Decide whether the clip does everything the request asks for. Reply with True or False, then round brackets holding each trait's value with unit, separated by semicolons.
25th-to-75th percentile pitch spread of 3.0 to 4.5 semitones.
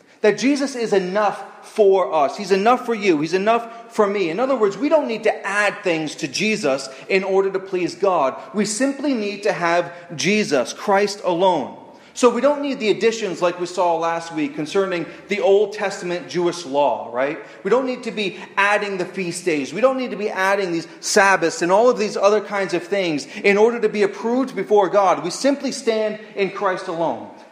True (3.8 semitones)